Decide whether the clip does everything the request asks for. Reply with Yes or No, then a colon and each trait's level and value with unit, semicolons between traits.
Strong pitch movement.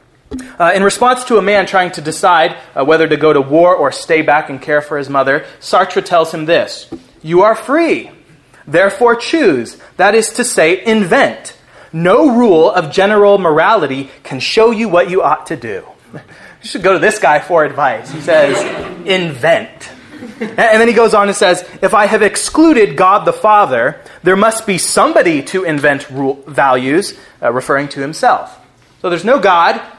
Yes: wide, 6.2 semitones